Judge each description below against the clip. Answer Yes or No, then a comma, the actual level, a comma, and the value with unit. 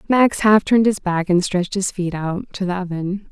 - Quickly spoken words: Yes, fast, 235 wpm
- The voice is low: No, high, 190 Hz